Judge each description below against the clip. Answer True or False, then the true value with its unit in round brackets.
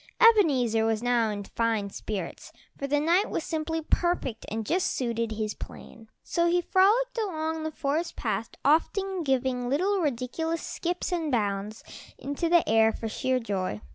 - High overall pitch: True (275 Hz)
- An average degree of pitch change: False (7.2 semitones)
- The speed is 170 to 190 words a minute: False (160 wpm)